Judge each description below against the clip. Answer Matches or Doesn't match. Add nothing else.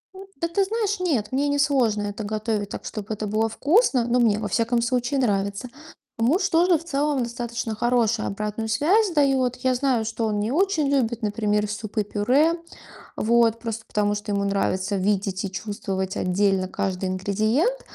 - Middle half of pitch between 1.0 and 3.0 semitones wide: Doesn't match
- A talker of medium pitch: Doesn't match